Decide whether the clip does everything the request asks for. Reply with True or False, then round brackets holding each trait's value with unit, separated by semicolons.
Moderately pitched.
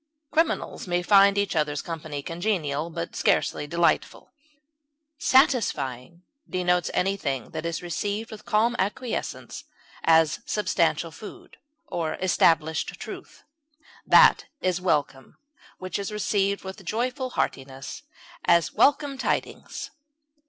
True (180 Hz)